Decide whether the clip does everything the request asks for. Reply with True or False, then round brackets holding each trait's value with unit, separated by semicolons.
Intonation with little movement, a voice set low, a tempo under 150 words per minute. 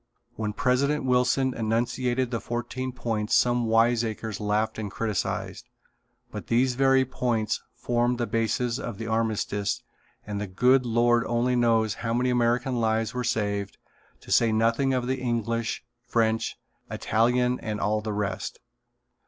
True (2.0 semitones; 115 Hz; 140 wpm)